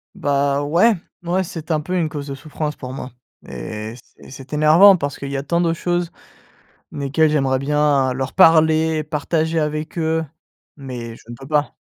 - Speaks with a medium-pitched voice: Yes, medium, 150 Hz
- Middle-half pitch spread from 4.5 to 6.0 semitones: No, average, 2.9 semitones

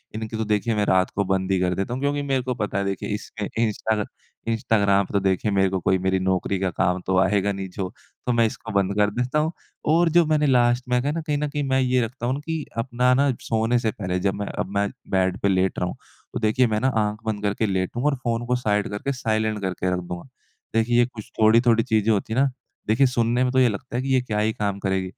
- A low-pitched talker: Yes, low, 110 Hz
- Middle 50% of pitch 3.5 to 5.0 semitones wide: Yes, average, 4.2 semitones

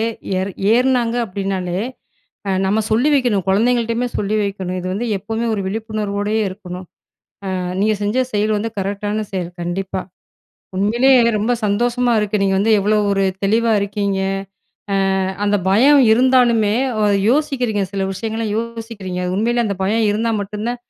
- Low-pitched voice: No, high, 210 Hz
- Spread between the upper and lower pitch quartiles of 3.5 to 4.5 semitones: No, average, 2.8 semitones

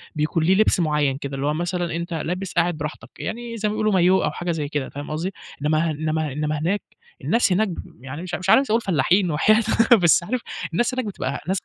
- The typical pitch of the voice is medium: Yes, medium, 170 Hz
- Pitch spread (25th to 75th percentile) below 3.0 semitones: No, average, 4.2 semitones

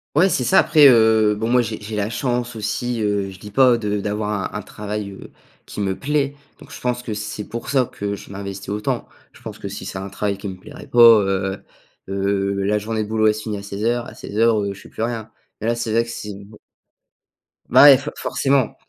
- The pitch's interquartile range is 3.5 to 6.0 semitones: No, average, 2.7 semitones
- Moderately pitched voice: No, low, 105 Hz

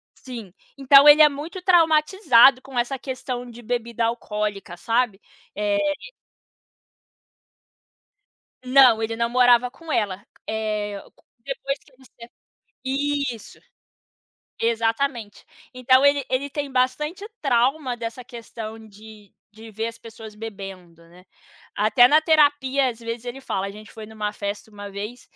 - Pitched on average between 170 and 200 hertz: No, high, 240 Hz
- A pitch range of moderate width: Yes, average, 4.0 semitones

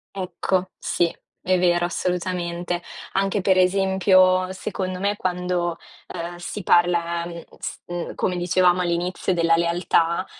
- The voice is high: No, medium, 180 Hz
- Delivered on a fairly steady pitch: Yes, narrow, 1.2 semitones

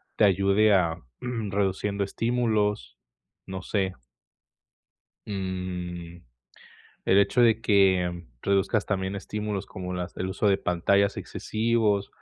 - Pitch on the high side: No, low, 100 Hz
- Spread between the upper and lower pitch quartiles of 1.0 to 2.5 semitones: Yes, narrow, 2.2 semitones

